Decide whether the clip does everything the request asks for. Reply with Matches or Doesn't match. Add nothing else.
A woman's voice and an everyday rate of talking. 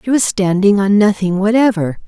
Matches